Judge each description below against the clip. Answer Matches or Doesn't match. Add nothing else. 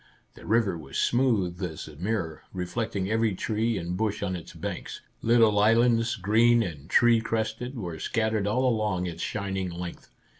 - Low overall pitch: Matches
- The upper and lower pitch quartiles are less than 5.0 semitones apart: Matches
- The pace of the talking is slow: Doesn't match